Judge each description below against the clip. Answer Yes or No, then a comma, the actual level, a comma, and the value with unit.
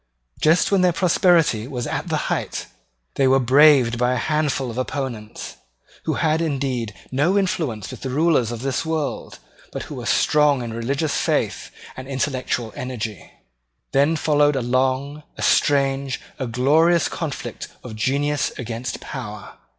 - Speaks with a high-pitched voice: No, low, 135 Hz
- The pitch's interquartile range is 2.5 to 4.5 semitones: Yes, average, 3.6 semitones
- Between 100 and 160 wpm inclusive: Yes, average, 150 wpm